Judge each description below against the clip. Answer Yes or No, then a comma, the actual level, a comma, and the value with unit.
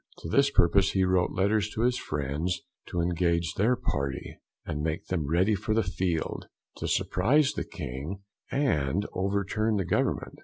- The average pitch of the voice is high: No, very low, 95 Hz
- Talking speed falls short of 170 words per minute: Yes, average, 160 wpm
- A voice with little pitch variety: No, average, 4.4 semitones